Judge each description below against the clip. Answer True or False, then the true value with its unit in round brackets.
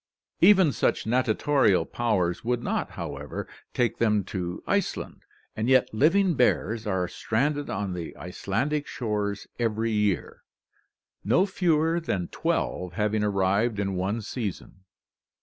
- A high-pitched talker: False (110 Hz)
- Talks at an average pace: False (125 wpm)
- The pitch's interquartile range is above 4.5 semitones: True (5.1 semitones)